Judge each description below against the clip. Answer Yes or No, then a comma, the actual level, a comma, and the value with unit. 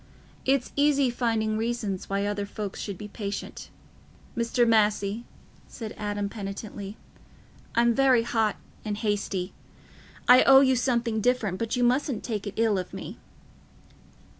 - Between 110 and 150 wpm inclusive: Yes, average, 140 wpm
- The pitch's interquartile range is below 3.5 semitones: Yes, average, 2.9 semitones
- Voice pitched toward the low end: No, high, 220 Hz